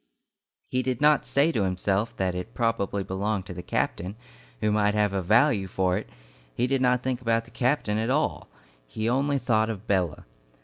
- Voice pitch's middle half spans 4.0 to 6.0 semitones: Yes, average, 4.5 semitones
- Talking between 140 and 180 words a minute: No, average, 190 wpm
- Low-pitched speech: Yes, low, 110 Hz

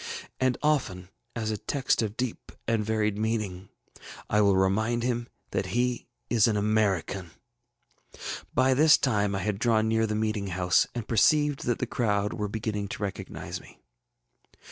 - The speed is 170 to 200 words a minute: No, average, 160 wpm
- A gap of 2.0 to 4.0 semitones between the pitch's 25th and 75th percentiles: Yes, average, 2.8 semitones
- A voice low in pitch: Yes, low, 110 Hz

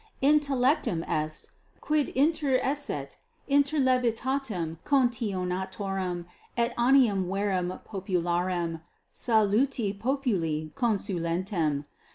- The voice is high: Yes, high, 205 Hz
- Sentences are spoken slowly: Yes, slow, 70 wpm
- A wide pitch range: Yes, wide, 6.8 semitones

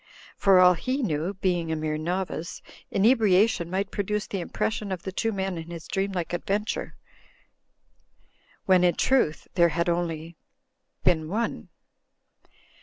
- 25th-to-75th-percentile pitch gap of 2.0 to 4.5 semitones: Yes, average, 3.0 semitones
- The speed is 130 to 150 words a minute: Yes, average, 145 wpm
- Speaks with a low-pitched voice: No, medium, 185 Hz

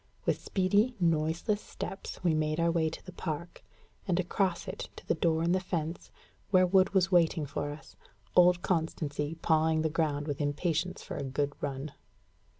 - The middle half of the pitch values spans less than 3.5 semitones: Yes, average, 2.9 semitones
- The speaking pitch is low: No, medium, 165 Hz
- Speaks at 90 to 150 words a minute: No, average, 175 wpm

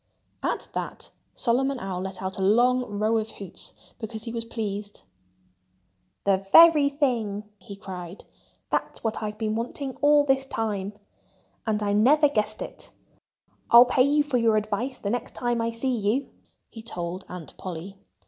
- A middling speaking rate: Yes, average, 160 wpm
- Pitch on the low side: No, high, 220 Hz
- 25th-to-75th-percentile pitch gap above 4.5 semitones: No, average, 3.8 semitones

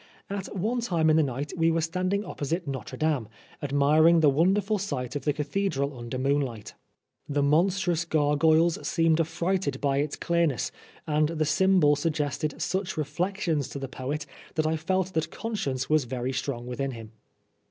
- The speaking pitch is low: No, medium, 155 Hz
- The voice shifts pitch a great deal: No, average, 3.5 semitones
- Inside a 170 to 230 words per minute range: Yes, average, 175 wpm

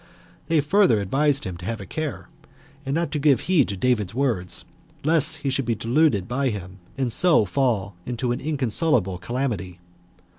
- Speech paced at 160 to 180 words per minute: Yes, average, 175 wpm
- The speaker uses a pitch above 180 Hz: No, low, 125 Hz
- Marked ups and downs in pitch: Yes, wide, 6.2 semitones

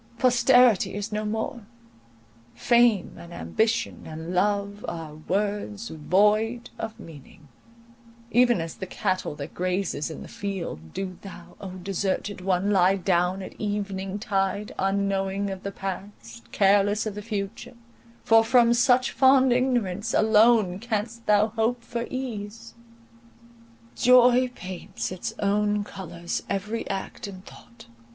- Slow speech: Yes, slow, 130 wpm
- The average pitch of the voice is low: No, high, 205 Hz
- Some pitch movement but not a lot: Yes, average, 3.3 semitones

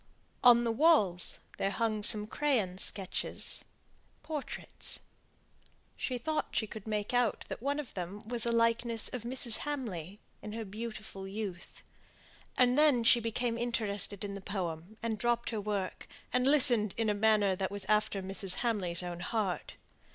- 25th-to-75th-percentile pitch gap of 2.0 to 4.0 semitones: Yes, average, 3.3 semitones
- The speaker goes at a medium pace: Yes, average, 160 wpm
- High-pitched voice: Yes, high, 220 Hz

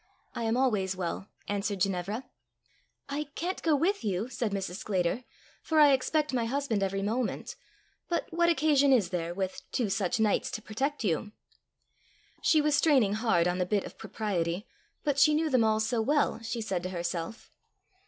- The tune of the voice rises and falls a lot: Yes, wide, 6.4 semitones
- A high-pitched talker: Yes, high, 220 Hz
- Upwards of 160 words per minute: Yes, average, 175 wpm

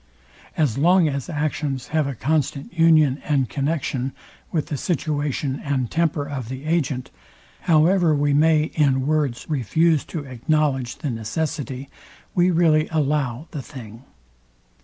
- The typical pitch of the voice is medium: Yes, medium, 145 Hz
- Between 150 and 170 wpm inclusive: No, slow, 135 wpm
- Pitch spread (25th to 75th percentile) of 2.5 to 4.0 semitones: Yes, average, 2.9 semitones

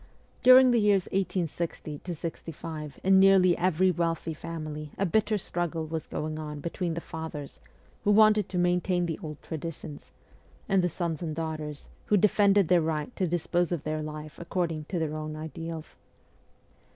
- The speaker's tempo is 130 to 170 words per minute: Yes, average, 160 wpm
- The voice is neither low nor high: Yes, medium, 165 Hz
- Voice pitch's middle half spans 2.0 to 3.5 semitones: Yes, average, 3.0 semitones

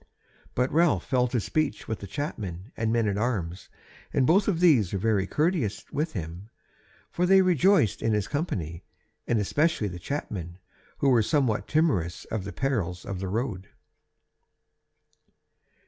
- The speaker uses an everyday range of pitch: No, wide, 7.4 semitones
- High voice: No, low, 115 Hz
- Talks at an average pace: Yes, average, 155 wpm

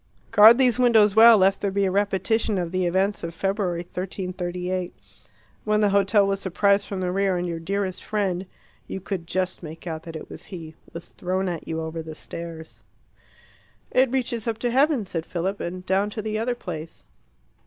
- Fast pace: No, average, 190 wpm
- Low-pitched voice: No, high, 190 Hz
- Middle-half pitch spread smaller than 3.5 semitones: Yes, average, 3.0 semitones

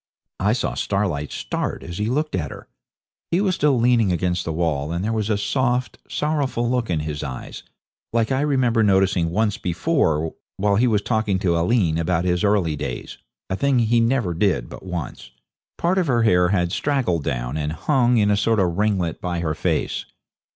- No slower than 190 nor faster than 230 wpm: Yes, average, 195 wpm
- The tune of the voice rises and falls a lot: Yes, wide, 5.9 semitones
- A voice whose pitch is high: No, low, 100 Hz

